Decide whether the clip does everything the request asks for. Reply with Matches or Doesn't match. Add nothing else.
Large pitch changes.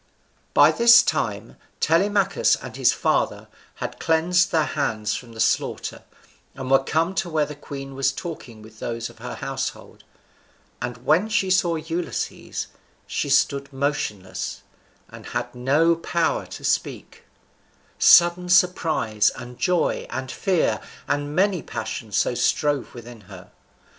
Matches